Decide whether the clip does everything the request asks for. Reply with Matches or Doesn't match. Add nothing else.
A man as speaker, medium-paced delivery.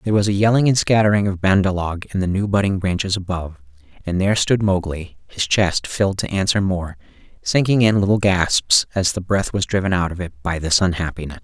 Doesn't match